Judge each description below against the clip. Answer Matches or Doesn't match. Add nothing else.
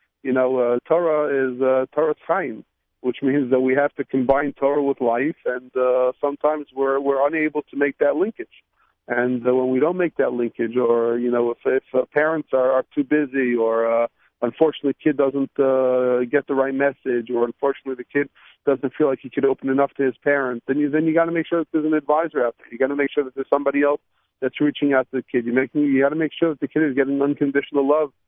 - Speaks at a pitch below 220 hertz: Matches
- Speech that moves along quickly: Matches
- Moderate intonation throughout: Doesn't match